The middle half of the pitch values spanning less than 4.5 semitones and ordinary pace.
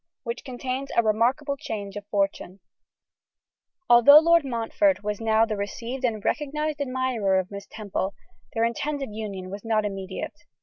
No: average, 5.1 semitones; average, 145 wpm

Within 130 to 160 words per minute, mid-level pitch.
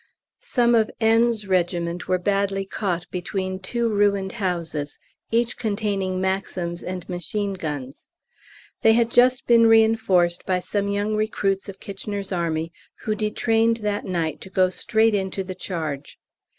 No: average, 140 wpm; high, 195 Hz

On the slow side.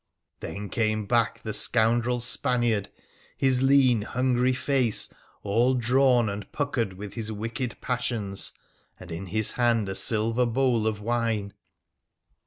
Yes: slow, 130 wpm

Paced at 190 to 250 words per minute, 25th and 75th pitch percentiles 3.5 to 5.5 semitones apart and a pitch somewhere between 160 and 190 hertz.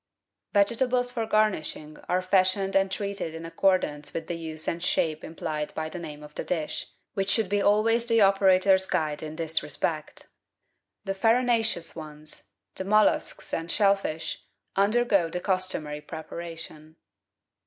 No: average, 150 wpm; average, 4.2 semitones; medium, 185 Hz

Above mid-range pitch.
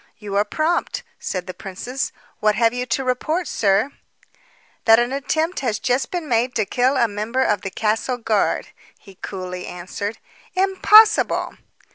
Yes: high, 230 Hz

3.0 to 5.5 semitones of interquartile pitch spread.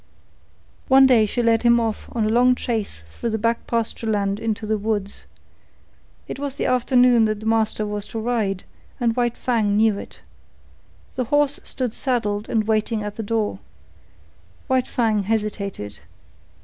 No: narrow, 2.4 semitones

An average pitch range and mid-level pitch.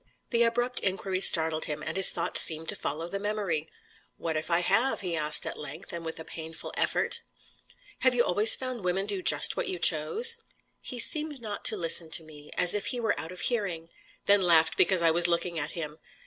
Yes: average, 4.5 semitones; medium, 175 Hz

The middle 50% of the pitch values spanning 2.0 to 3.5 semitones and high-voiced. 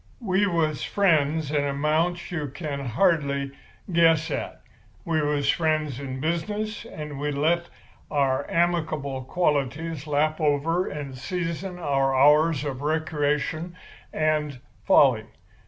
No: average, 2.9 semitones; medium, 155 Hz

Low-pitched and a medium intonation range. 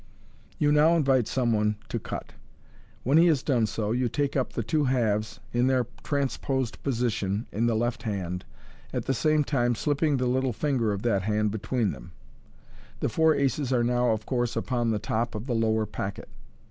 Yes: low, 120 Hz; average, 3.6 semitones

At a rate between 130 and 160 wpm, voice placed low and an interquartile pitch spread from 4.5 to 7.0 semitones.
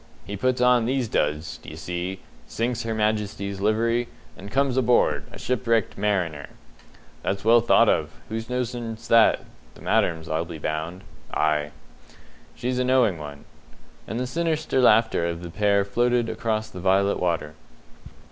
Yes: average, 150 wpm; low, 110 Hz; wide, 5.4 semitones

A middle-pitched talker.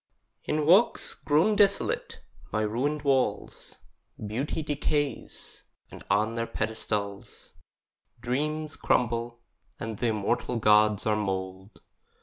No: low, 115 Hz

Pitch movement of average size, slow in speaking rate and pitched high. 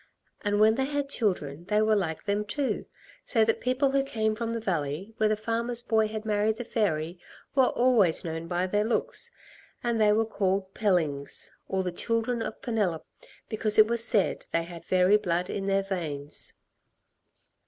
No: average, 4.0 semitones; average, 180 wpm; high, 210 Hz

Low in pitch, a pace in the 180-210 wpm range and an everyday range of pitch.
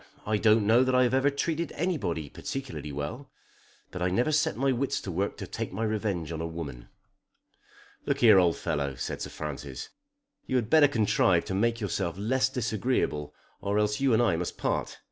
No: low, 110 Hz; average, 190 wpm; wide, 7.0 semitones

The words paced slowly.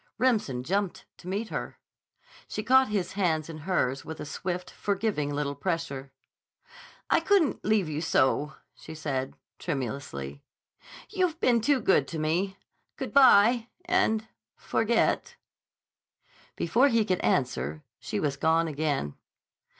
Yes: slow, 125 wpm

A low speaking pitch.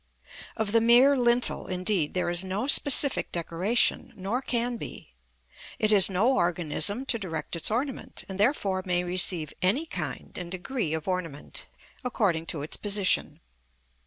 No: high, 195 Hz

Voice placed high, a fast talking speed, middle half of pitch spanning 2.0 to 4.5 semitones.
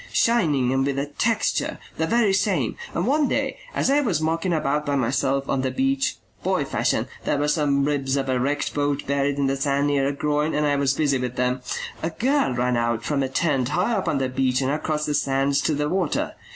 No: medium, 145 Hz; fast, 230 wpm; average, 2.8 semitones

